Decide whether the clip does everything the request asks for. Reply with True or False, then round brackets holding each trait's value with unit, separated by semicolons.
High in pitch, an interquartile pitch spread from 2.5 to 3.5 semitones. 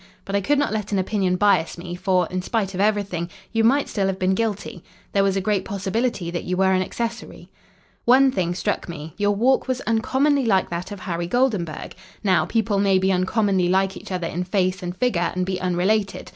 True (195 Hz; 3.0 semitones)